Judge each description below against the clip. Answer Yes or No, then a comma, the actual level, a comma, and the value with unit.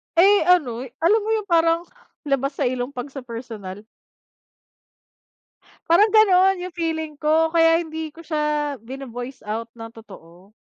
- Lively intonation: Yes, wide, 5.7 semitones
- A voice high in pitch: Yes, very high, 300 Hz